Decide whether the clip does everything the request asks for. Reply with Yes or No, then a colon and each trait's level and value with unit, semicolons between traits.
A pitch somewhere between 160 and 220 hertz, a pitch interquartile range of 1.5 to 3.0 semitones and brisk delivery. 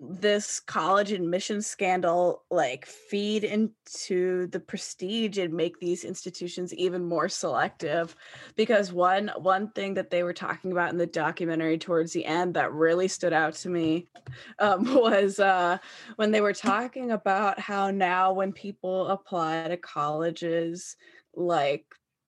No: medium, 185 Hz; average, 2.7 semitones; average, 145 wpm